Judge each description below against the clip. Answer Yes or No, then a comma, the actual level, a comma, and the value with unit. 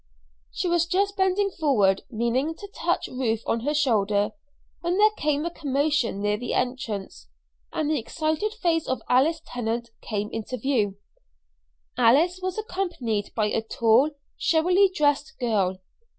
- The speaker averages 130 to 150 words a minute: Yes, average, 145 wpm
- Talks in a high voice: Yes, very high, 275 Hz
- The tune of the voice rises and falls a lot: Yes, wide, 7.2 semitones